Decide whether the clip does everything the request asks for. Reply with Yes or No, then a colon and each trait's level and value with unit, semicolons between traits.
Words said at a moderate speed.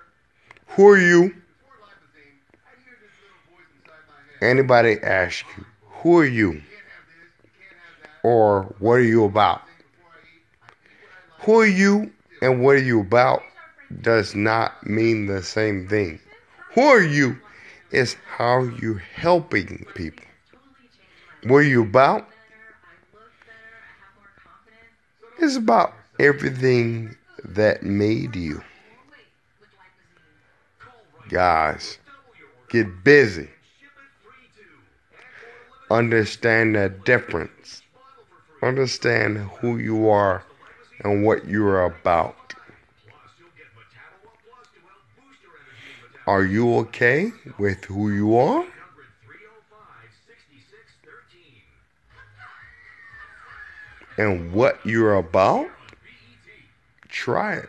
No: slow, 80 wpm